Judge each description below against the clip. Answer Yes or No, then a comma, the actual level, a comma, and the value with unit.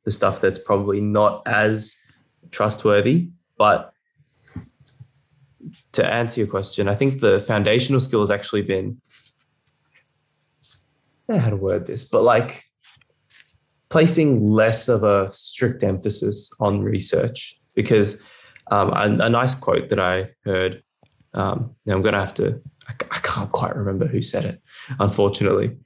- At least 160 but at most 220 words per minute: No, average, 140 wpm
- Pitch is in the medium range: No, low, 110 Hz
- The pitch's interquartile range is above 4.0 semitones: Yes, average, 4.4 semitones